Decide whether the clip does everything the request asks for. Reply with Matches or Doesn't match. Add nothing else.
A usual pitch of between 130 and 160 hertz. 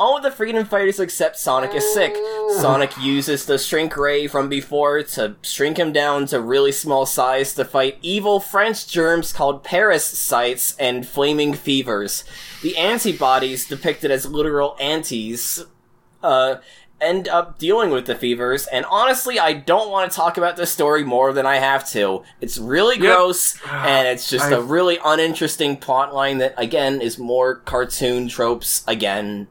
Matches